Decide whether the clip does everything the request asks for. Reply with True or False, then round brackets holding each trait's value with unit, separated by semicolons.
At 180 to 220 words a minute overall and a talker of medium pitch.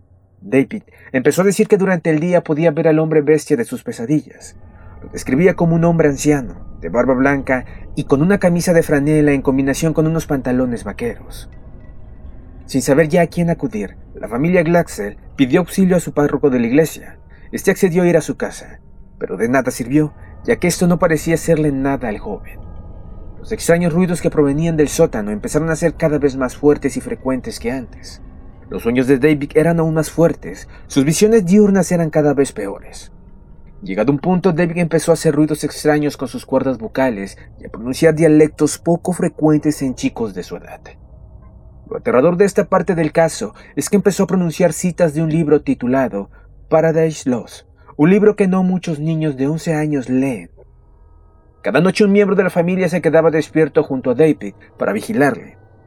True (190 wpm; 155 Hz)